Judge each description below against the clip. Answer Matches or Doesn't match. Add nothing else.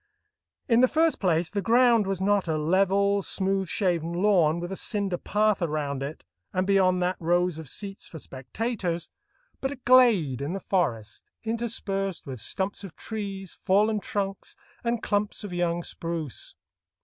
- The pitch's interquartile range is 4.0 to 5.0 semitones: Doesn't match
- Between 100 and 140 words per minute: Doesn't match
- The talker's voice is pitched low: Doesn't match